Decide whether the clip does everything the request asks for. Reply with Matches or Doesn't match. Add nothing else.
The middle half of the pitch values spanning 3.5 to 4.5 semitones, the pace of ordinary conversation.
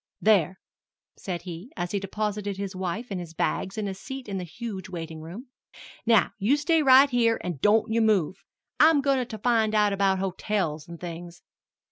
Matches